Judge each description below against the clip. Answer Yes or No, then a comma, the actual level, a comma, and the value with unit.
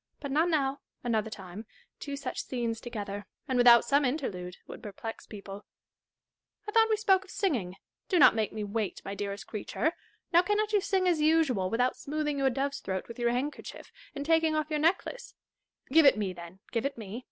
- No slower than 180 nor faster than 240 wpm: Yes, average, 200 wpm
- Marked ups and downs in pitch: Yes, wide, 6.7 semitones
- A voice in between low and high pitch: No, very high, 255 Hz